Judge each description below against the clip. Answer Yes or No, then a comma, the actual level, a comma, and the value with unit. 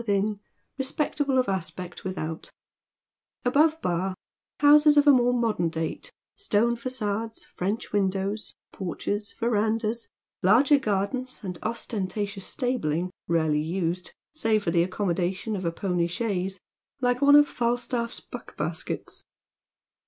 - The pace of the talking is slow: Yes, slow, 120 wpm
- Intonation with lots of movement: No, average, 5.0 semitones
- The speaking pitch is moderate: No, high, 210 Hz